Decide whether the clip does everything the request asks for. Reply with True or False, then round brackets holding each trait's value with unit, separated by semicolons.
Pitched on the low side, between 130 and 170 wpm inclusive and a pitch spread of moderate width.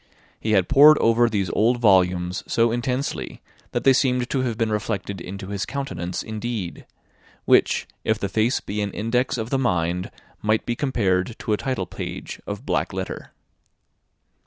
True (110 Hz; 165 wpm; 4.0 semitones)